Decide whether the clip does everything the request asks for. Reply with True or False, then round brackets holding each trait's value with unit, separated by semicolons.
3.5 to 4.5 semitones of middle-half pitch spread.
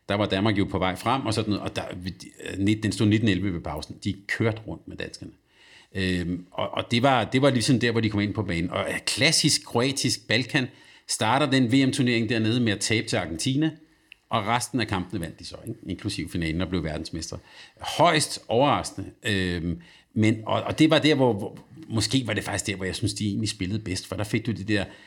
True (4.2 semitones)